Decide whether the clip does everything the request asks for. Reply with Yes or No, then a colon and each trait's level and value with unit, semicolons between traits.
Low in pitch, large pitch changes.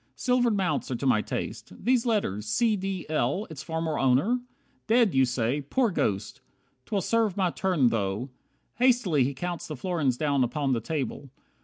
No: medium, 155 Hz; wide, 7.7 semitones